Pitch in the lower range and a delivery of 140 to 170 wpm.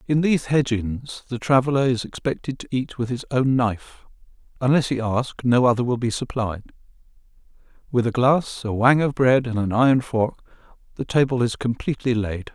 No: low, 125 Hz; average, 180 wpm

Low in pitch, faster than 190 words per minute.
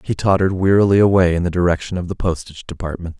Yes: very low, 90 Hz; fast, 205 wpm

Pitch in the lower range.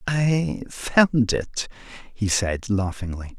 Yes: low, 115 Hz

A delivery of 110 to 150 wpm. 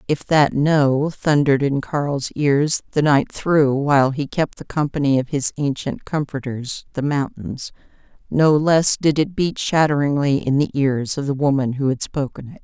No: average, 175 wpm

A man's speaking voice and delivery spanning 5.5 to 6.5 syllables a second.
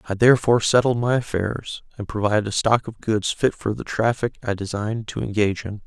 Yes: male; 5.9 syllables/s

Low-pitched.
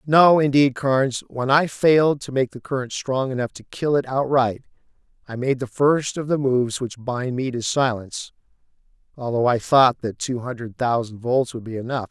Yes: low, 130 Hz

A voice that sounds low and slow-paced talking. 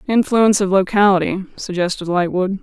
No: high, 195 Hz; slow, 115 wpm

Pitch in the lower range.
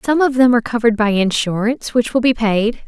No: high, 230 Hz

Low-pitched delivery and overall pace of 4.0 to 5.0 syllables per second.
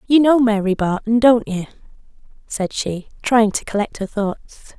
No: high, 220 Hz; 4.8 syllables/s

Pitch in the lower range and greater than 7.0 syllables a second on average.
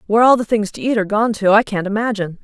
No: high, 215 Hz; 7.5 syllables/s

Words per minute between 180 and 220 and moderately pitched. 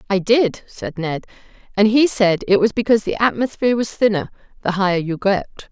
No: average, 190 wpm; high, 205 Hz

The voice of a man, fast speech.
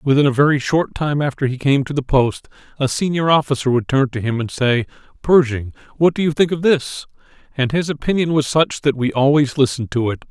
Yes: male; fast, 220 wpm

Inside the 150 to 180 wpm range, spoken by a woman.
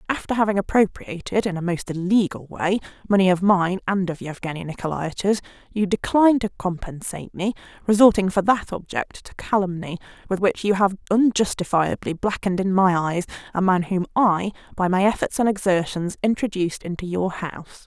Yes: average, 160 wpm; female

